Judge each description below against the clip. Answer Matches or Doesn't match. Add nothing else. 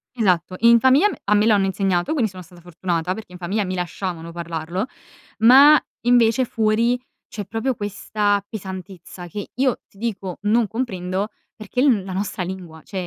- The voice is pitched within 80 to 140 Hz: Doesn't match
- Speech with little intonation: Doesn't match